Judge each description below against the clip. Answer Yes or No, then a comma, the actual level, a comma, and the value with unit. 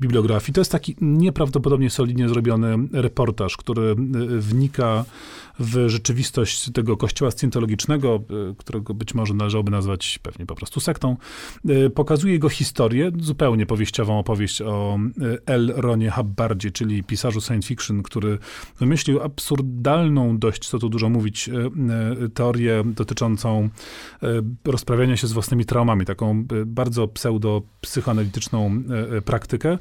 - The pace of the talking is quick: No, average, 115 wpm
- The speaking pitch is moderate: No, low, 115 Hz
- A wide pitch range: No, average, 3.0 semitones